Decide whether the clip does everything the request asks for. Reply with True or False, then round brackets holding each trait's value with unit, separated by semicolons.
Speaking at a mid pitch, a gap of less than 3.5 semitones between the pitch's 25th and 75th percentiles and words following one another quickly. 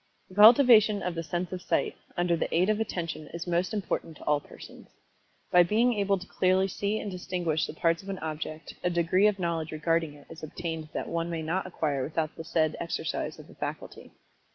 True (170 Hz; 2.9 semitones; 210 wpm)